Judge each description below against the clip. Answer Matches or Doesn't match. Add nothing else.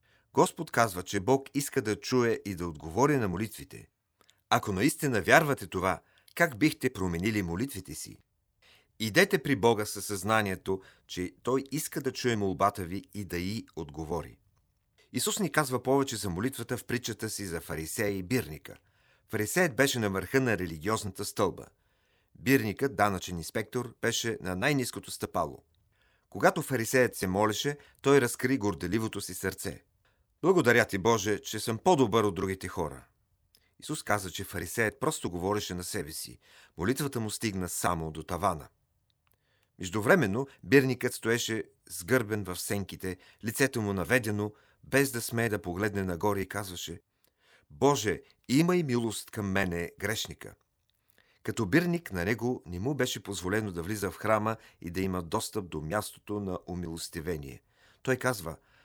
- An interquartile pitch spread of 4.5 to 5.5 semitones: Matches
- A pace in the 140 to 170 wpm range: Matches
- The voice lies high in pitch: Doesn't match